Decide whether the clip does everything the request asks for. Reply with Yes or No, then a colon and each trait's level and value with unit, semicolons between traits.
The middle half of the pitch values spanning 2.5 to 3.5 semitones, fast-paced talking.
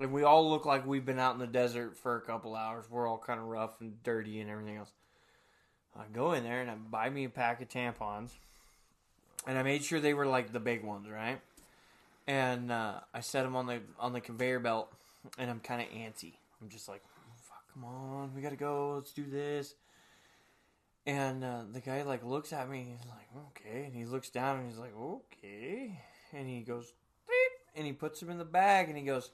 Yes: average, 3.0 semitones; fast, 230 wpm